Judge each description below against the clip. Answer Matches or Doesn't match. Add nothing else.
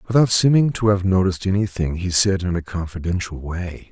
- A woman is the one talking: Doesn't match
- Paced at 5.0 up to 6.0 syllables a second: Matches